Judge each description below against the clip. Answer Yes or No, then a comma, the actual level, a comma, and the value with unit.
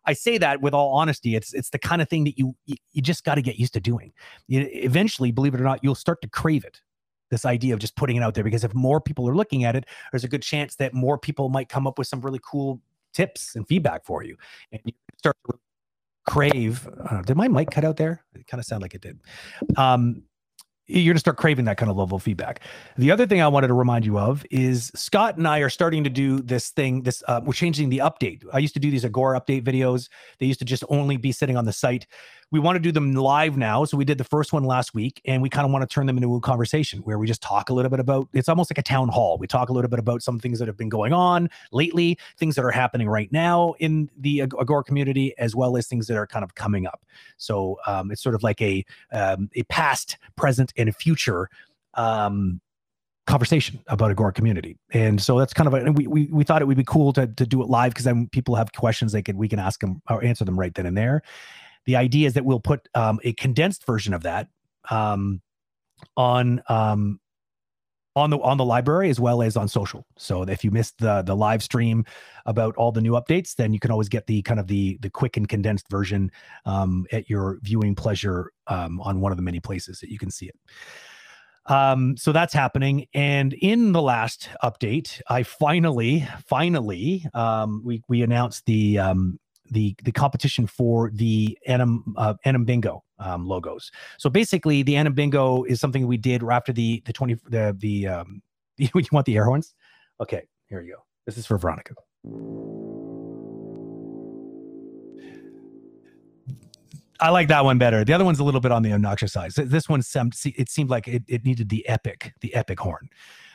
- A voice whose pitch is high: No, low, 125 Hz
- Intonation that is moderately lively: Yes, average, 4.5 semitones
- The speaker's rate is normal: No, fast, 225 wpm